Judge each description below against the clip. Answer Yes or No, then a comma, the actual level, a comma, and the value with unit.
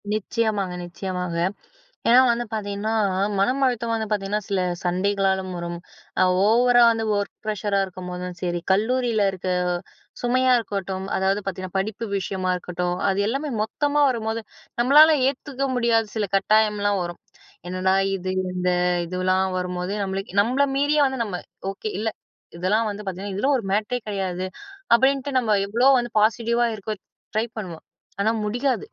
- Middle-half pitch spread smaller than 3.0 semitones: No, average, 3.9 semitones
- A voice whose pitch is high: Yes, high, 205 Hz